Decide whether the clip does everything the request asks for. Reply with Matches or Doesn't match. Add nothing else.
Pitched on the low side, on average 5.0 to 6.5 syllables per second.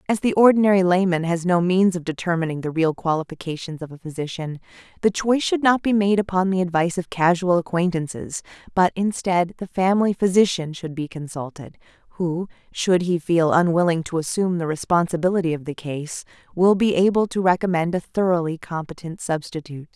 Doesn't match